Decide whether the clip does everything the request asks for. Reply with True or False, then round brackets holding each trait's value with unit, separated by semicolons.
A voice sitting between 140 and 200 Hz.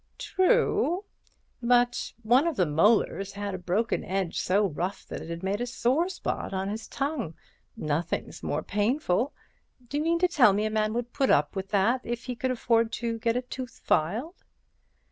False (230 Hz)